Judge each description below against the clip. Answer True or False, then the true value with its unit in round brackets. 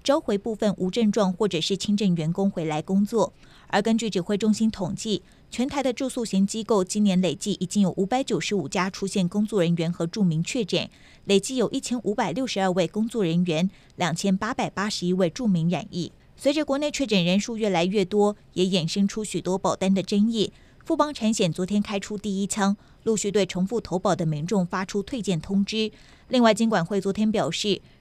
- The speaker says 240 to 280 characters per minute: False (310 characters per minute)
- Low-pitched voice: False (200 Hz)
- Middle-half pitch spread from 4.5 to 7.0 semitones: False (2.9 semitones)